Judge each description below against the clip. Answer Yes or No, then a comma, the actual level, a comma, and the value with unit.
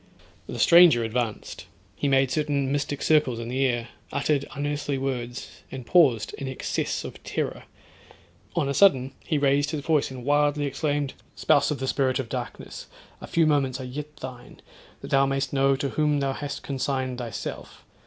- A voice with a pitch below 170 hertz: Yes, low, 135 Hz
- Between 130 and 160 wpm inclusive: No, average, 170 wpm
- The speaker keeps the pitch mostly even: Yes, narrow, 2.1 semitones